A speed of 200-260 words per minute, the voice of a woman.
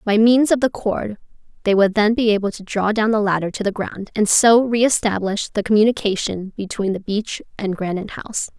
Yes: fast, 205 wpm; female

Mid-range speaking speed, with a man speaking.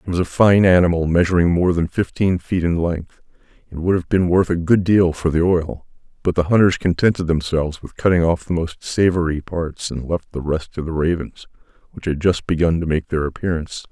No: fast, 215 wpm; male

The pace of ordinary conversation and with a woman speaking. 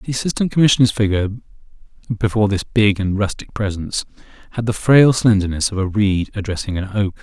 No: average, 165 wpm; male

